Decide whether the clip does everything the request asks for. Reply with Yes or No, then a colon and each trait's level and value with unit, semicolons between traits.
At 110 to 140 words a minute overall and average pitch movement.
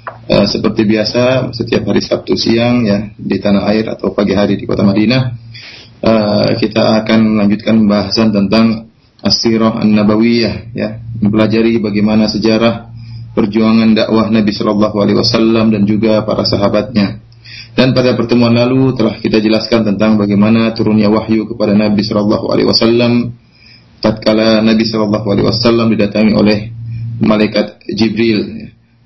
No: average, 135 wpm; narrow, 1.5 semitones